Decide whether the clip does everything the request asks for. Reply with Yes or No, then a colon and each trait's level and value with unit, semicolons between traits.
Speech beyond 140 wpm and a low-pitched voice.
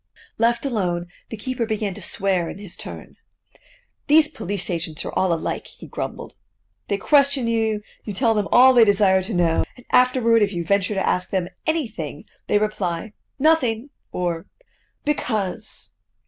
No: average, 160 wpm; high, 210 Hz